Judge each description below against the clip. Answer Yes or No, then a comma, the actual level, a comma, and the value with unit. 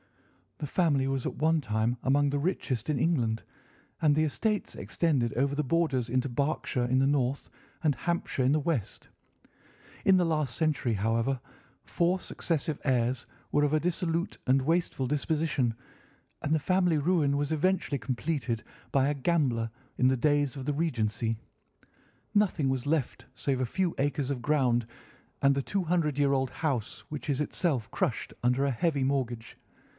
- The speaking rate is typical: Yes, average, 165 wpm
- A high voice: No, medium, 140 Hz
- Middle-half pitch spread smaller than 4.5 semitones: Yes, average, 3.7 semitones